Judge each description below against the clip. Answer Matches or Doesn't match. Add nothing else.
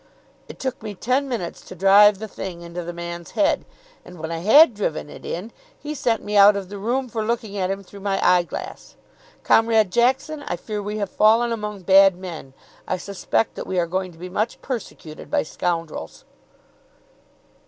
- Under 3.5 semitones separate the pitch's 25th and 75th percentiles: Doesn't match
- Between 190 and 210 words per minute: Matches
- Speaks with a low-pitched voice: Doesn't match